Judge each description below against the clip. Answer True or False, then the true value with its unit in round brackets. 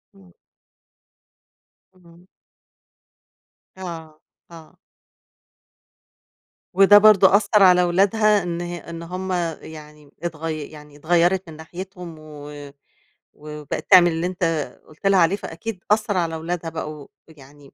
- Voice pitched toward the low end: False (170 Hz)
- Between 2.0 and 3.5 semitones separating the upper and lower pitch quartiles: True (3.2 semitones)